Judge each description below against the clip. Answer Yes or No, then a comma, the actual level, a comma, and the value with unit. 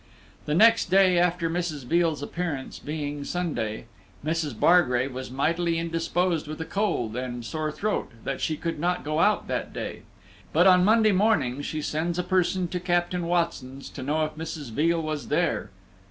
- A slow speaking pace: No, average, 170 wpm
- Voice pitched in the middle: Yes, medium, 165 Hz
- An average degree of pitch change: Yes, average, 3.4 semitones